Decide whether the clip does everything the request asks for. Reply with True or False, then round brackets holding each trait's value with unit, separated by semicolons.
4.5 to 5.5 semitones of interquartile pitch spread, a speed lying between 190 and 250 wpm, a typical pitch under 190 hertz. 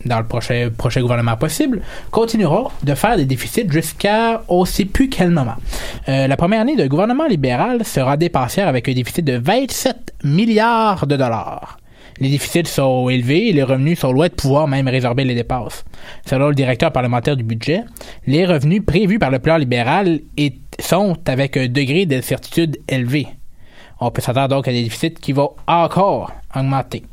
False (5.2 semitones; 175 wpm; 140 Hz)